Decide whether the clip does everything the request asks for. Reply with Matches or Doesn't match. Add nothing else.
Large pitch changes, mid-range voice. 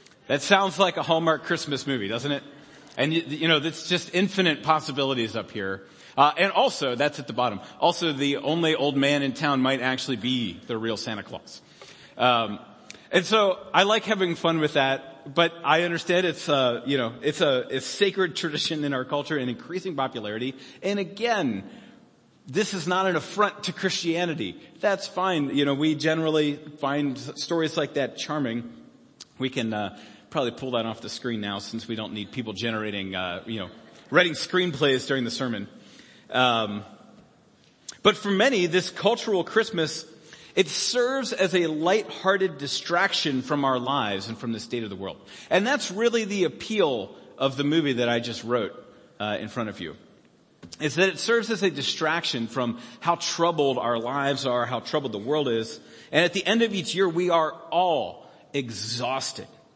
Matches